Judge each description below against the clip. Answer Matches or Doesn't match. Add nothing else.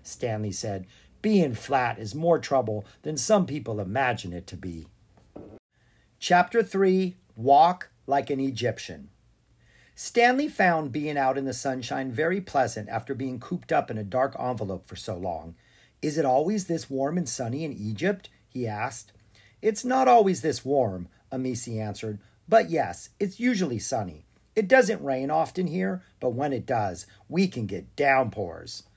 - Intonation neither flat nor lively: Doesn't match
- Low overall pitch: Matches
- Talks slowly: Doesn't match